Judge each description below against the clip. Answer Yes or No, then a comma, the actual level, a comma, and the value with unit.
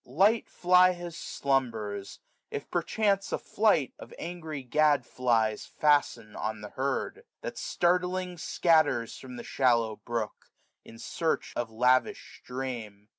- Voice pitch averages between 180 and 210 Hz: No, low, 135 Hz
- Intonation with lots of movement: Yes, wide, 7.0 semitones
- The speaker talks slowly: Yes, slow, 130 wpm